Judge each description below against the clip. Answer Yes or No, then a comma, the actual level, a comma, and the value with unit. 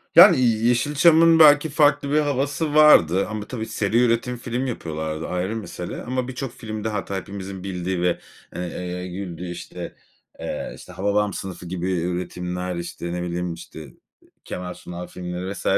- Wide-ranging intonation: Yes, wide, 5.7 semitones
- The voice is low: Yes, very low, 95 Hz